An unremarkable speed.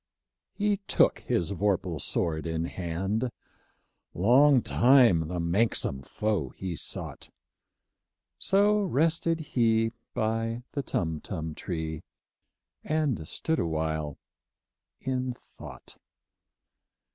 No: slow, 90 wpm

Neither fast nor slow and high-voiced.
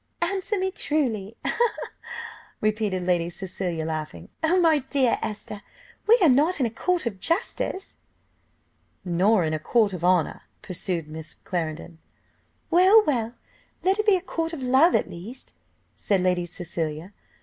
Yes: average, 145 wpm; high, 215 Hz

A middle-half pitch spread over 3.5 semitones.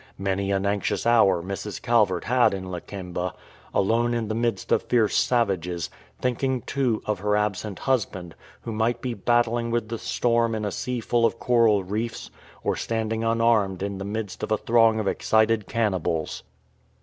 No: average, 3.1 semitones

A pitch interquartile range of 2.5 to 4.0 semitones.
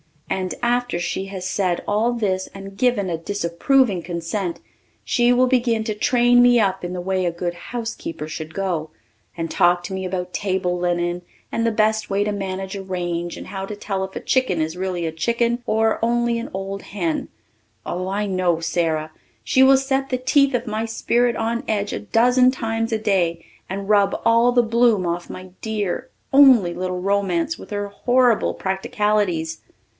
No: average, 4.6 semitones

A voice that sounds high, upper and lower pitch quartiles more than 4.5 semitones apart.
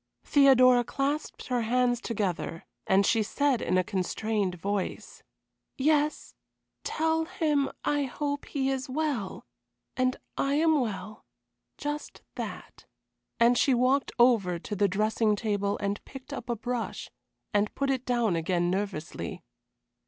Yes: high, 240 Hz; average, 5.3 semitones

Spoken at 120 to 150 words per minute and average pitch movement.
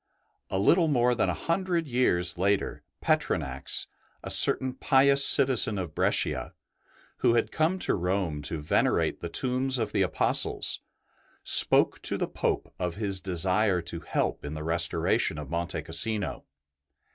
No: average, 145 wpm; wide, 7.1 semitones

